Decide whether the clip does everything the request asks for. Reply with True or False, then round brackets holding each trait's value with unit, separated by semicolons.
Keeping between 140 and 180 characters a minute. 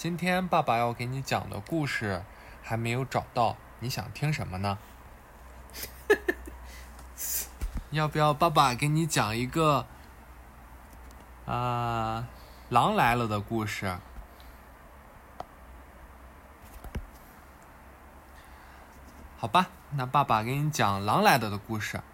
True (145 characters per minute)